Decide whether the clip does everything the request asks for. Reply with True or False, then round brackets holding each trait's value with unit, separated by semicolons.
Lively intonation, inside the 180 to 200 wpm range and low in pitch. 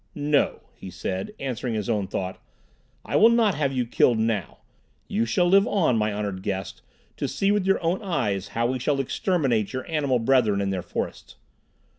True (6.8 semitones; 185 wpm; 125 Hz)